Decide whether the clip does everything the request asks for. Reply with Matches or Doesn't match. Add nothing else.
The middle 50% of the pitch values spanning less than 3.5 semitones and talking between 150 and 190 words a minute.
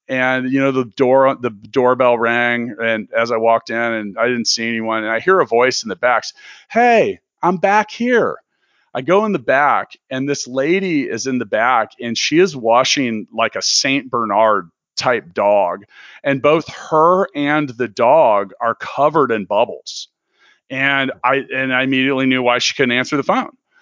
Doesn't match